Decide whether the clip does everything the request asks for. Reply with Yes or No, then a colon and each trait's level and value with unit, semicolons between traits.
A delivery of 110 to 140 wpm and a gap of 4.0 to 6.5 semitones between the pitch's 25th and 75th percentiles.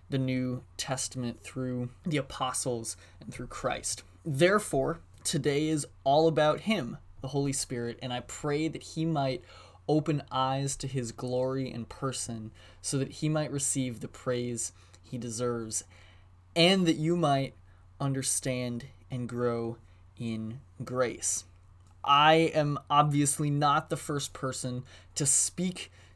Yes: slow, 135 wpm; average, 4.8 semitones